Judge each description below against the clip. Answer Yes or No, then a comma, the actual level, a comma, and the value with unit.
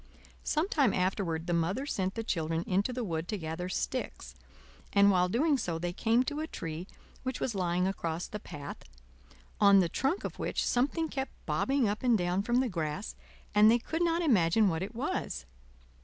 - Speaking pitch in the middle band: No, high, 200 Hz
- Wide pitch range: Yes, wide, 6.6 semitones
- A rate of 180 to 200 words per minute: Yes, average, 190 wpm